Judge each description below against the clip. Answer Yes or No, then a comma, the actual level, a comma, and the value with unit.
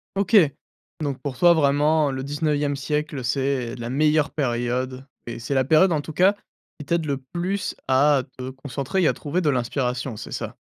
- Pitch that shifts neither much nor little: Yes, average, 3.0 semitones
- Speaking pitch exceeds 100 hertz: Yes, medium, 140 Hz